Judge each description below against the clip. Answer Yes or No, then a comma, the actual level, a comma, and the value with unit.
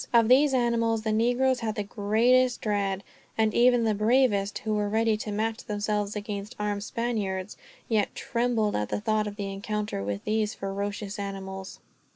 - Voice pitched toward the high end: Yes, high, 215 Hz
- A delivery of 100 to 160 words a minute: No, average, 170 wpm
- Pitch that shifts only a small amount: Yes, narrow, 2.1 semitones